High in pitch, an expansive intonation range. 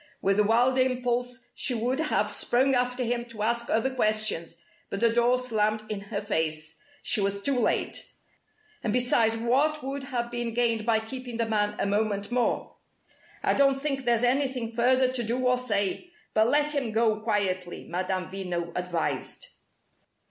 No: high, 235 Hz; average, 3.2 semitones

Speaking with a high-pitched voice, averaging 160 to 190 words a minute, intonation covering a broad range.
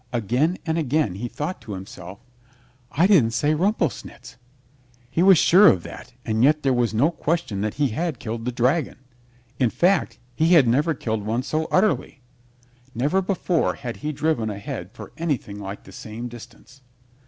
No: low, 130 Hz; average, 175 wpm; wide, 6.2 semitones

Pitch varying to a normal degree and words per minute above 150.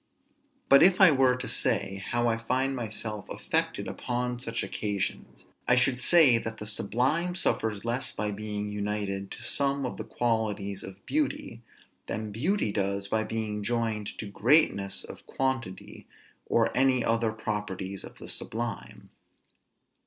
No: average, 3.4 semitones; average, 145 wpm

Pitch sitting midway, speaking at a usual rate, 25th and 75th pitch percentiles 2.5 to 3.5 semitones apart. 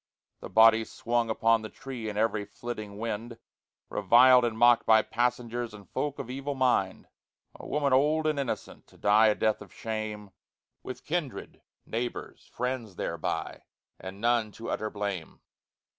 No: low, 115 Hz; average, 155 wpm; average, 2.8 semitones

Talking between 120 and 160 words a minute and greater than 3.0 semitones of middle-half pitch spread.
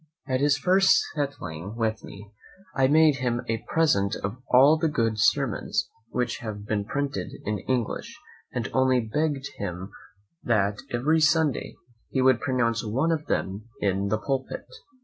Yes: average, 155 wpm; average, 5.3 semitones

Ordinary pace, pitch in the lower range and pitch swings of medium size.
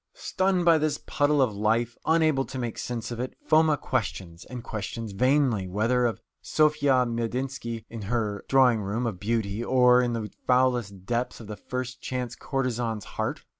Yes: average, 170 wpm; low, 120 Hz; average, 3.1 semitones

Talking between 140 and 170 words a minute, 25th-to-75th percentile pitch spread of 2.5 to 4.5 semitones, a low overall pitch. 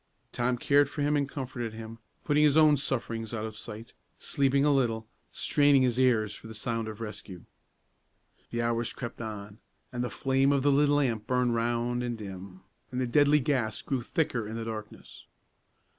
No: average, 185 wpm; average, 3.7 semitones; low, 120 Hz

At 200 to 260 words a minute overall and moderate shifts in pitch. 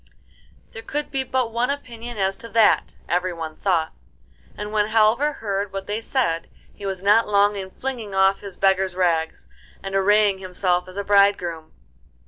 No: average, 165 wpm; average, 3.1 semitones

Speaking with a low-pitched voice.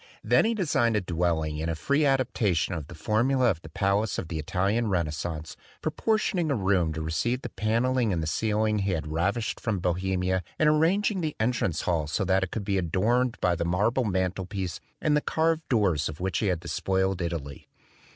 Yes: very low, 95 Hz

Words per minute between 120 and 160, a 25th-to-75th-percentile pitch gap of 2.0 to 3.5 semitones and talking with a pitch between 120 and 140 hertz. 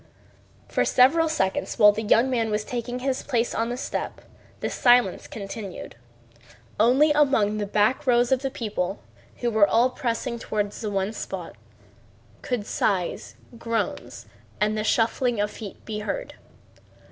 No: average, 150 wpm; average, 3.2 semitones; high, 230 Hz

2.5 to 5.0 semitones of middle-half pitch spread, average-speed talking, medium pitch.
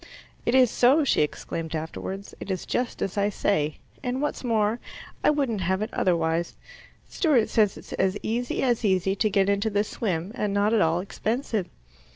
No: average, 4.0 semitones; average, 185 wpm; high, 205 Hz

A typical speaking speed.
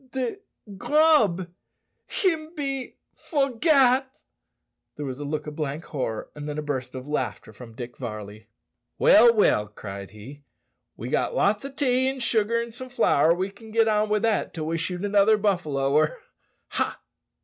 Yes: average, 170 wpm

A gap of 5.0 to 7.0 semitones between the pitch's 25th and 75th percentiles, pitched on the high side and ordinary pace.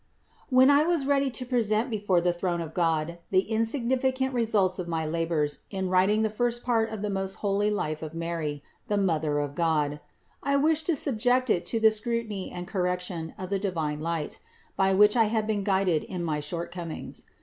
Yes: average, 5.3 semitones; high, 195 Hz; average, 195 wpm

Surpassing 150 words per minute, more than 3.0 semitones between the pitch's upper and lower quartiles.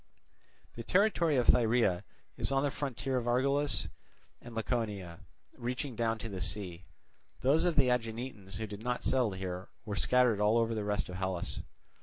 Yes: average, 165 wpm; average, 4.0 semitones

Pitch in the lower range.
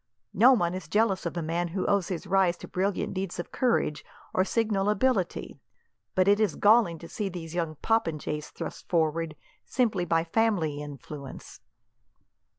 No: medium, 180 Hz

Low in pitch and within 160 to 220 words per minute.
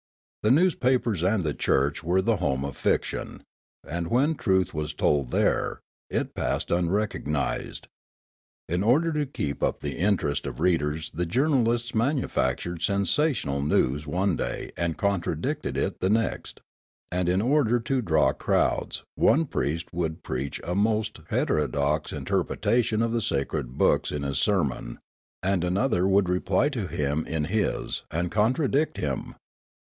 No: very low, 90 Hz; average, 145 wpm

